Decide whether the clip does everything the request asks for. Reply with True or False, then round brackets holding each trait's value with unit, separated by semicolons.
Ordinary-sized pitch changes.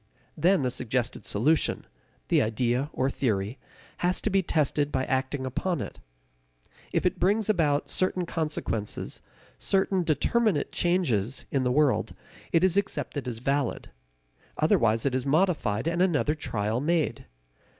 False (5.7 semitones)